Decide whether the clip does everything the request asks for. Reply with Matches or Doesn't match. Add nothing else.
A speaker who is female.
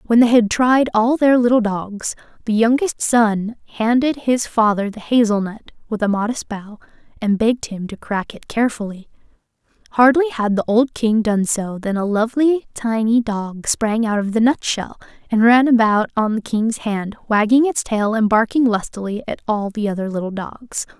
Matches